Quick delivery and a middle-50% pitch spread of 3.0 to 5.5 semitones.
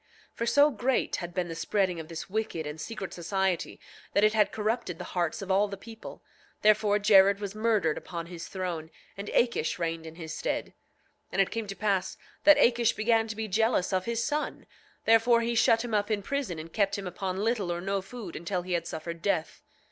Yes: fast, 215 wpm; average, 4.2 semitones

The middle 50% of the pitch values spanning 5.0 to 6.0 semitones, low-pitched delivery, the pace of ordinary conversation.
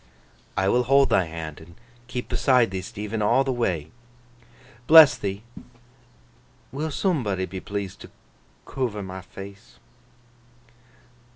No: average, 5.3 semitones; low, 100 Hz; slow, 120 wpm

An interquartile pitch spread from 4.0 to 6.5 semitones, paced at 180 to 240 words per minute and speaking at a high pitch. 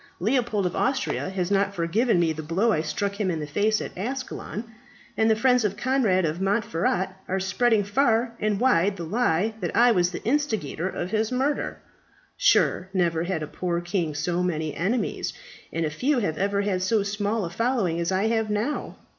Yes: average, 4.5 semitones; average, 190 wpm; high, 200 Hz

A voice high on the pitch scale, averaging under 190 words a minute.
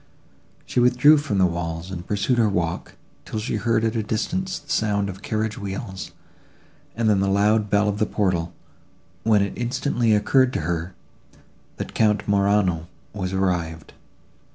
No: low, 105 Hz; average, 160 wpm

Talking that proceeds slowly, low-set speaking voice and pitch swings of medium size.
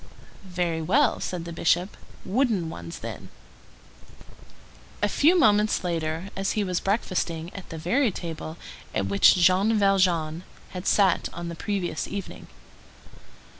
No: slow, 130 wpm; medium, 180 Hz; average, 3.4 semitones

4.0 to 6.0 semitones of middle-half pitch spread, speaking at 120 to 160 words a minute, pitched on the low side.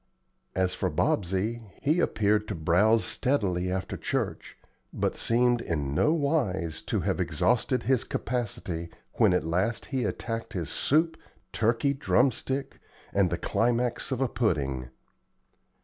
Yes: wide, 5.6 semitones; slow, 135 wpm; low, 110 Hz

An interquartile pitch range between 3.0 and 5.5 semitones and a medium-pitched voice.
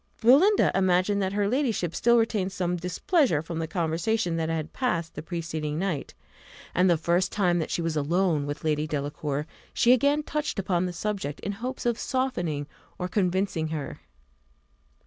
Yes: average, 4.7 semitones; medium, 180 Hz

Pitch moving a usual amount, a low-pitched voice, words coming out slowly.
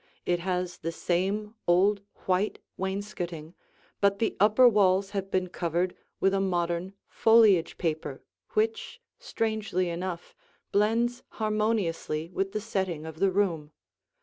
No: average, 3.4 semitones; high, 190 Hz; slow, 125 wpm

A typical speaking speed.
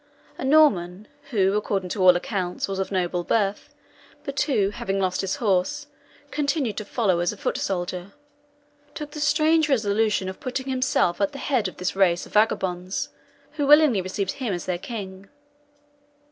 Yes: average, 170 wpm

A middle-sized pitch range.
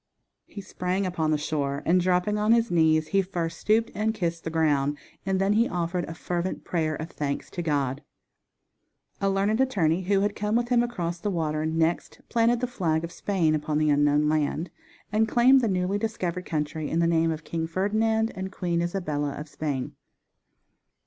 Yes: average, 4.4 semitones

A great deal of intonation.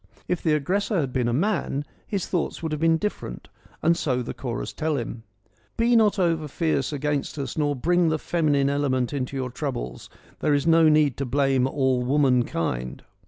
No: average, 4.0 semitones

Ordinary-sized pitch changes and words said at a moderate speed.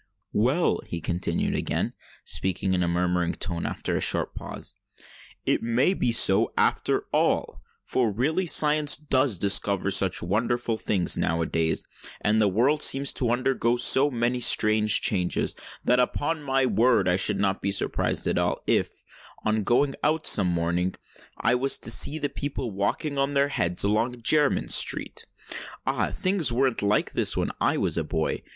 No: wide, 6.0 semitones; average, 170 wpm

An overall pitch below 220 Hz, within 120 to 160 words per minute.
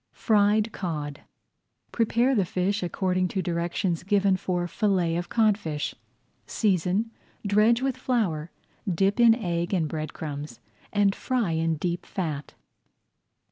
Yes: medium, 185 Hz; slow, 135 wpm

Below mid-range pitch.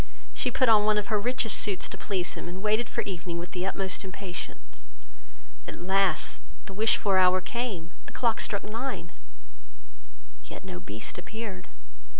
No: high, 195 Hz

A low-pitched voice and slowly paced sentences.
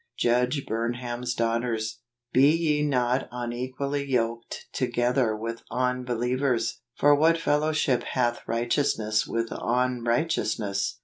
Yes: low, 125 Hz; slow, 110 wpm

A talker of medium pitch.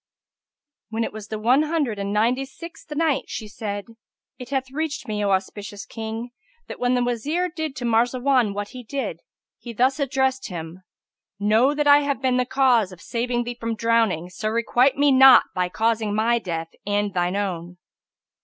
No: high, 235 Hz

